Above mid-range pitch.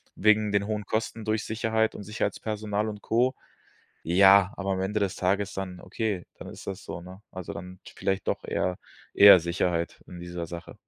No: low, 100 Hz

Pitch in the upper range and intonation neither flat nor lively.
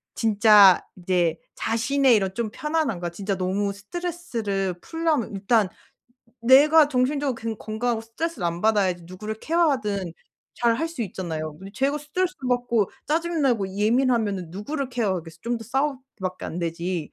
No: high, 225 Hz; wide, 6.2 semitones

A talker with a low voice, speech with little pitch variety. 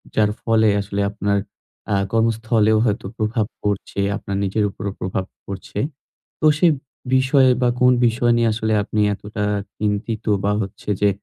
Yes: low, 110 Hz; narrow, 2.0 semitones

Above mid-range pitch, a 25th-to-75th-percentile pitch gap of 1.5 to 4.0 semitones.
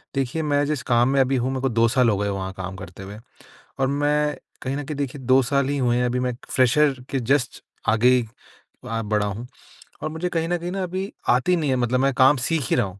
No: low, 130 Hz; average, 3.5 semitones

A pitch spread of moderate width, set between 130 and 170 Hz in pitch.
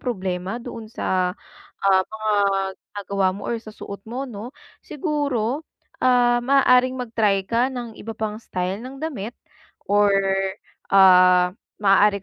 No: average, 4.0 semitones; high, 215 Hz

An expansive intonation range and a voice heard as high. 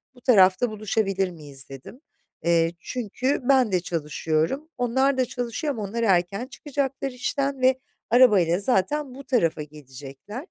Yes: wide, 7.2 semitones; high, 220 Hz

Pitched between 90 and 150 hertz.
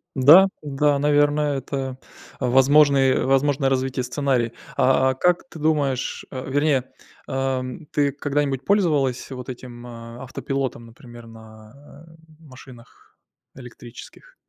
Yes: low, 135 Hz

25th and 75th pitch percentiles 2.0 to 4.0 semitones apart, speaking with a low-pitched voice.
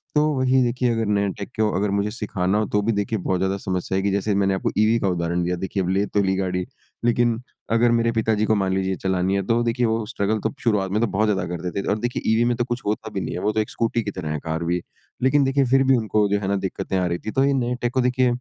Yes: average, 3.6 semitones; low, 105 Hz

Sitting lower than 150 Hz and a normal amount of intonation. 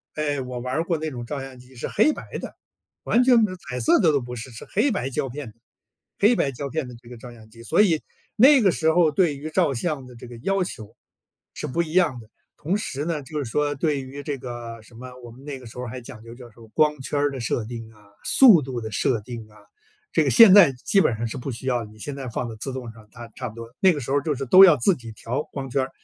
Yes: low, 135 Hz; average, 4.7 semitones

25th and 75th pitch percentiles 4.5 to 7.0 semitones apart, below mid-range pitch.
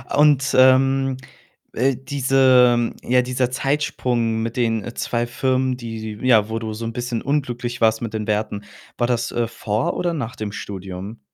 No: narrow, 2.6 semitones; low, 120 Hz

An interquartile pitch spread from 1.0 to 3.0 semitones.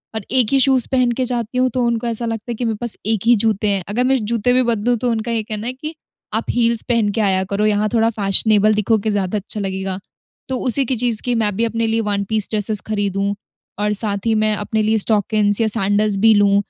Yes: narrow, 2.4 semitones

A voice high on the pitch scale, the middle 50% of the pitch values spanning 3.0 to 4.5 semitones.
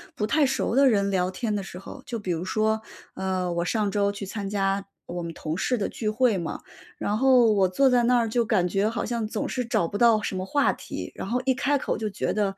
Yes: high, 210 Hz; average, 3.6 semitones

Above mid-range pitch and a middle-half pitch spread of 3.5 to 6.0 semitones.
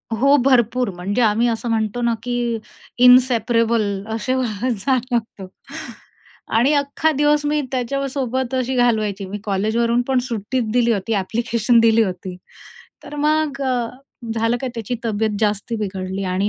No: high, 235 Hz; average, 3.1 semitones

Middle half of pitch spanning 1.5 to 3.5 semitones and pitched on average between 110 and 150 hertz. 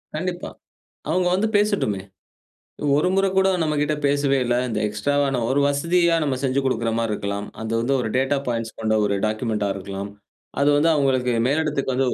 No: average, 5.3 semitones; low, 135 Hz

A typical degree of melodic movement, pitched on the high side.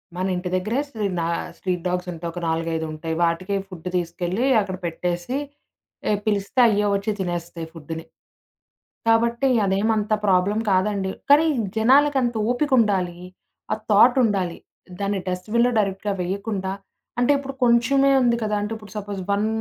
Yes: average, 4.1 semitones; high, 200 Hz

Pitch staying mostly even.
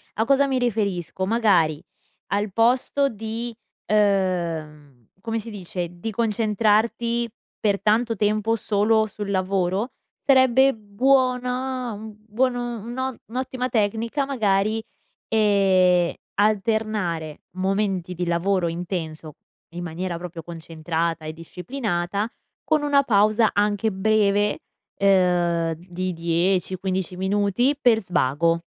No: average, 4.3 semitones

